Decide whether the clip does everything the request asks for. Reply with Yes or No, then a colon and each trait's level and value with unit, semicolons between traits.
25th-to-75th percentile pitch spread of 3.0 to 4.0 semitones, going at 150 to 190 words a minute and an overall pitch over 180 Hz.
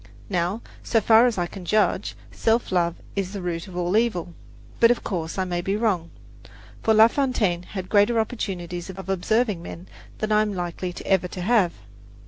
Yes: average, 3.7 semitones; average, 185 wpm; high, 190 Hz